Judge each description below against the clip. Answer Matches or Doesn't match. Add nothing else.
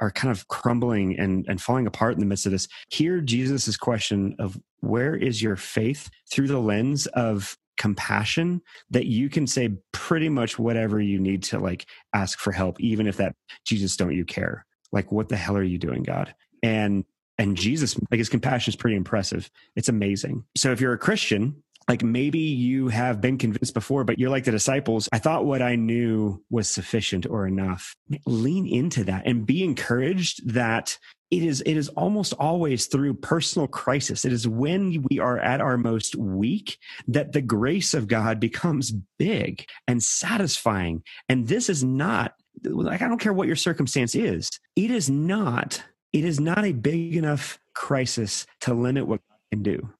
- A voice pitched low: Matches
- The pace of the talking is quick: Doesn't match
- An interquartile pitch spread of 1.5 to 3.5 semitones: Doesn't match